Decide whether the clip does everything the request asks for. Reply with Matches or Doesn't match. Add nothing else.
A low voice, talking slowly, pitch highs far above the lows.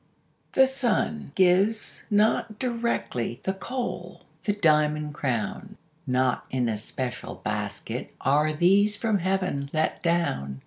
Doesn't match